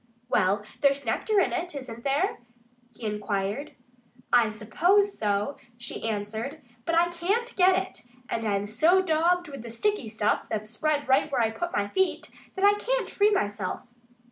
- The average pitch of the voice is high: Yes, very high, 280 Hz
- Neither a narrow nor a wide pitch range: No, wide, 8.7 semitones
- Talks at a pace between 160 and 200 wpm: Yes, average, 170 wpm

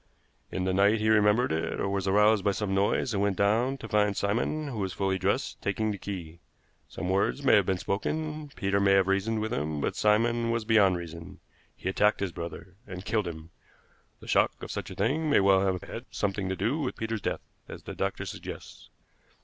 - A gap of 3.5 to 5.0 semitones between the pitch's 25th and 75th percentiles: No, average, 2.7 semitones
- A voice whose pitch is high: No, low, 100 Hz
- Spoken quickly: Yes, fast, 215 wpm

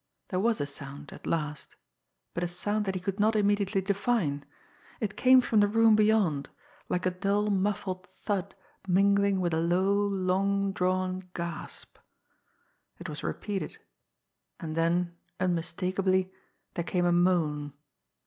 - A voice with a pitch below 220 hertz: Yes, medium, 185 Hz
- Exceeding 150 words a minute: No, average, 140 wpm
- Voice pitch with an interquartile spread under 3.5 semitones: Yes, narrow, 2.6 semitones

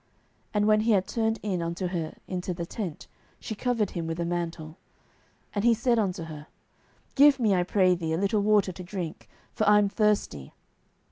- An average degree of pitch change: Yes, average, 3.8 semitones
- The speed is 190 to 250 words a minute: Yes, average, 200 wpm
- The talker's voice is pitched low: No, high, 190 Hz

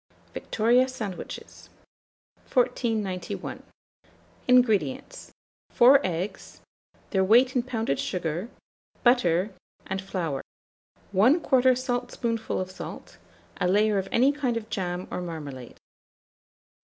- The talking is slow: Yes, slow, 95 wpm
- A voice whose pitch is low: No, high, 220 Hz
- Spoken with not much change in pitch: No, average, 5.3 semitones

